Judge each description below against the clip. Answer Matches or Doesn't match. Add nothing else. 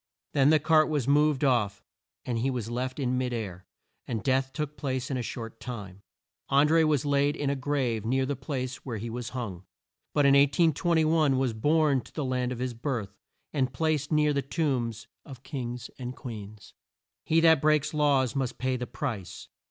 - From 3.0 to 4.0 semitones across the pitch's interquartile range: Matches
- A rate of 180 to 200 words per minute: Matches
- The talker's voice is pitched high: Doesn't match